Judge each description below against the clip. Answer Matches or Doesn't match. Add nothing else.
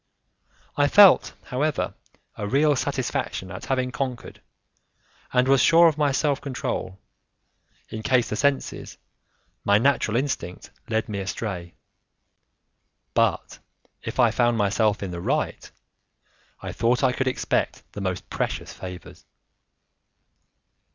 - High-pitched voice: Doesn't match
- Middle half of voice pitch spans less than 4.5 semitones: Doesn't match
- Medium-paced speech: Doesn't match